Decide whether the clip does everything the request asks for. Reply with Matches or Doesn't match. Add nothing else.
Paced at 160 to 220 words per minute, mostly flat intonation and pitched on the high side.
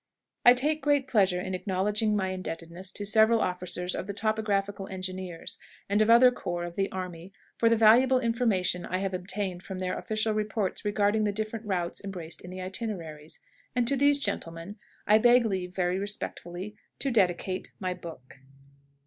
Doesn't match